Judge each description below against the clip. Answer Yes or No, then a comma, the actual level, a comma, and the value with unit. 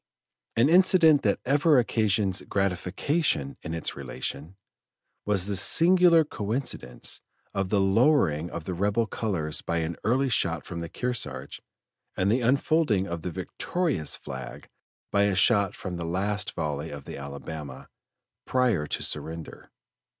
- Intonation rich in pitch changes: Yes, wide, 7.1 semitones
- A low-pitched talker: Yes, low, 100 Hz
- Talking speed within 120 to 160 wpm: Yes, average, 140 wpm